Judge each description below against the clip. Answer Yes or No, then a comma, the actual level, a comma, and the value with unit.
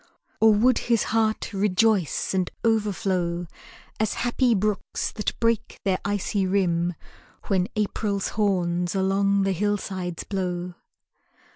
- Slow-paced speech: Yes, slow, 115 wpm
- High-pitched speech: Yes, high, 195 Hz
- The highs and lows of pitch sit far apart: No, average, 2.7 semitones